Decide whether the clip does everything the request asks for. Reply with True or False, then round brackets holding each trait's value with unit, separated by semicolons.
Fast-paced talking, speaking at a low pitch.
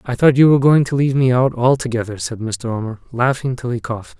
True (245 wpm; 125 Hz)